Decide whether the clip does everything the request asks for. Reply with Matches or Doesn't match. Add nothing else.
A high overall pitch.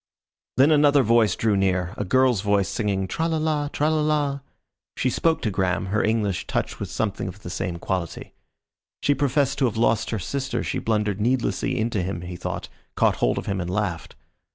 Doesn't match